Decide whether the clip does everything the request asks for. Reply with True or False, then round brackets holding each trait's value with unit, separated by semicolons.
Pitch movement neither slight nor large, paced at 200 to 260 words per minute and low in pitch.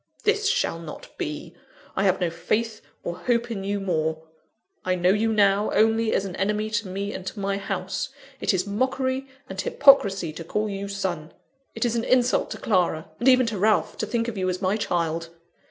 False (3.7 semitones; 205 wpm; 200 Hz)